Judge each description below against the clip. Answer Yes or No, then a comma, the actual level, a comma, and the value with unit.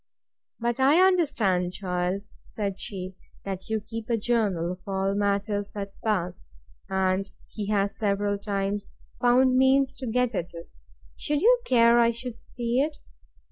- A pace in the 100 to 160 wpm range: Yes, average, 150 wpm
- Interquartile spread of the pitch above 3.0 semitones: Yes, average, 3.8 semitones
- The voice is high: Yes, high, 210 Hz